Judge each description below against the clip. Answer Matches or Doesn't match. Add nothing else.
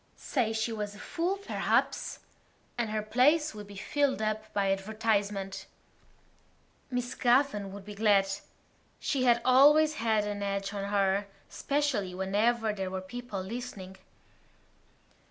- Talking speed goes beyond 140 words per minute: Doesn't match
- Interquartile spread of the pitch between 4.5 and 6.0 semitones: Doesn't match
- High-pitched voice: Matches